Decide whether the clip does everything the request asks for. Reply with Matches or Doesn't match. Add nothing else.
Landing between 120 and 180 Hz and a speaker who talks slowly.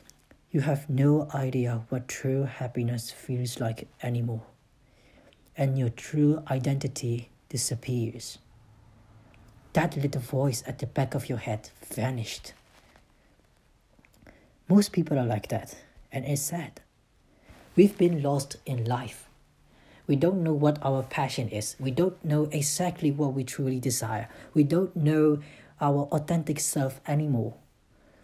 Matches